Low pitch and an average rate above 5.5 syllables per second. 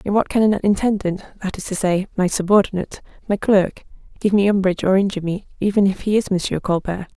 No: high, 195 Hz; 6.2 syllables/s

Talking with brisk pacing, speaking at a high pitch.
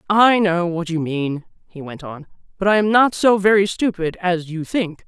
No: fast, 215 wpm; medium, 180 Hz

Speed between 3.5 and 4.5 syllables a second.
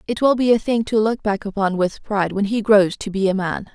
No: 5.6 syllables/s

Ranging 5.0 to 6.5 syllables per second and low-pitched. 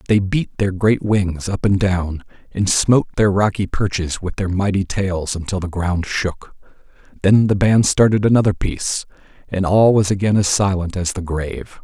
No: 4.8 syllables/s; very low, 95 Hz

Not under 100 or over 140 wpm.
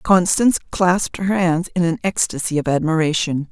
No: average, 155 wpm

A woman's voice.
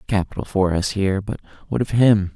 No: male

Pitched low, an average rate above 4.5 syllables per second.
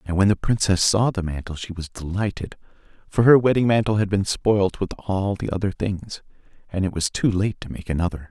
Yes: very low, 95 Hz; 5.4 syllables/s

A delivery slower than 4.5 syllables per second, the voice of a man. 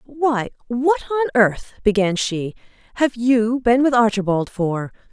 No: 4.0 syllables/s; female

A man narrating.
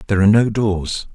Yes: male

